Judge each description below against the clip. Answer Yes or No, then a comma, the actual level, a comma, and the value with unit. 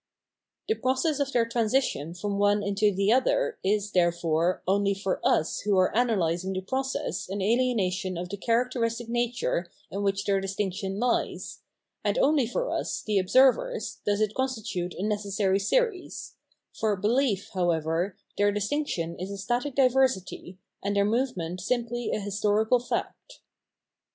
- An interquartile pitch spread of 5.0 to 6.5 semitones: No, average, 4.4 semitones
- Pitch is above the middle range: Yes, high, 205 Hz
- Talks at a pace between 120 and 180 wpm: Yes, average, 145 wpm